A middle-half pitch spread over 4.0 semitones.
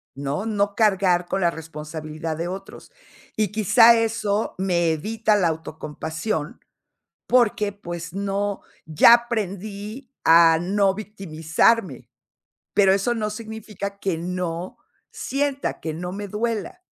Yes: average, 4.4 semitones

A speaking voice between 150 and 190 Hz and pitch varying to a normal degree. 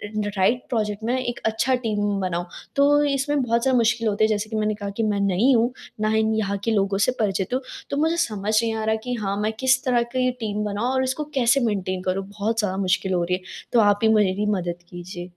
No: high, 215 Hz; average, 3.4 semitones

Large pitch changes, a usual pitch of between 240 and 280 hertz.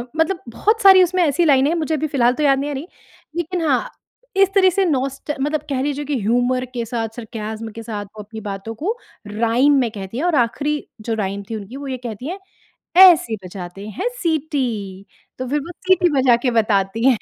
Yes: wide, 5.9 semitones; very high, 260 Hz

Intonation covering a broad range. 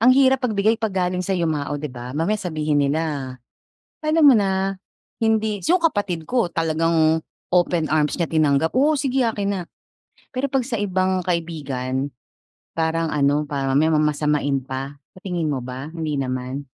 Yes: wide, 5.8 semitones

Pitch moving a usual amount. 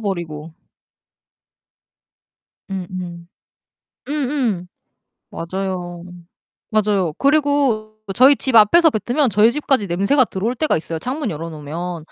No: wide, 7.0 semitones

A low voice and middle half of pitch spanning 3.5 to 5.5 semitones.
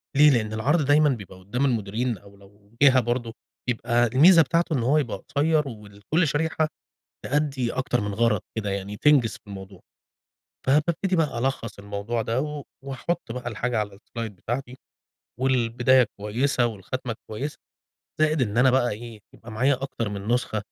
Yes: low, 120 Hz; average, 4.6 semitones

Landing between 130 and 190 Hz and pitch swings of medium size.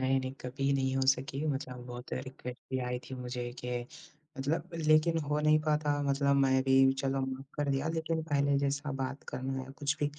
No: low, 135 Hz; narrow, 1.9 semitones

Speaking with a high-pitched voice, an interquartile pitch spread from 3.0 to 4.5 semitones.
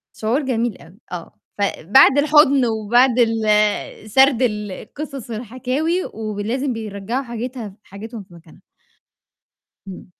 Yes: high, 225 Hz; average, 3.8 semitones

